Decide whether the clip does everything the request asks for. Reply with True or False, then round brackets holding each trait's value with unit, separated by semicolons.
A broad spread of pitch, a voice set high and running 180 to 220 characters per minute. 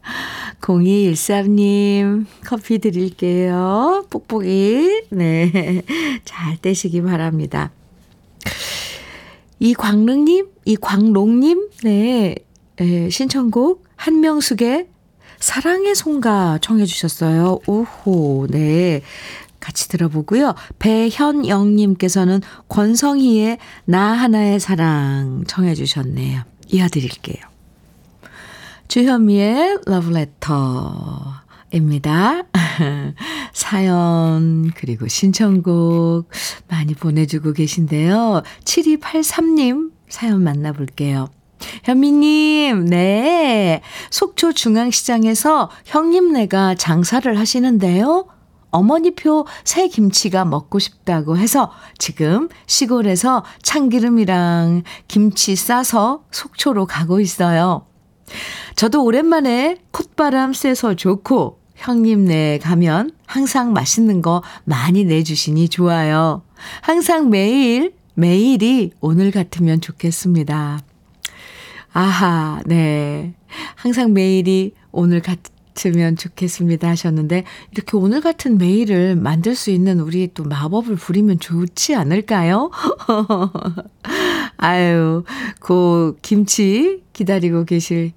True (6.3 semitones; 195 Hz; 200 characters per minute)